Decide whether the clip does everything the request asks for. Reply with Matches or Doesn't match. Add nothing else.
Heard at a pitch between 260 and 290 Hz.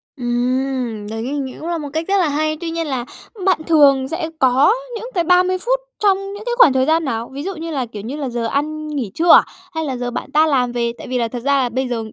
Matches